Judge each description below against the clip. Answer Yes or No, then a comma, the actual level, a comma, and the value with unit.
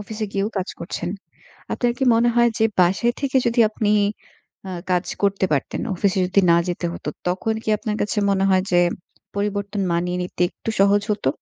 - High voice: Yes, high, 200 Hz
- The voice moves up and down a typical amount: Yes, average, 3.2 semitones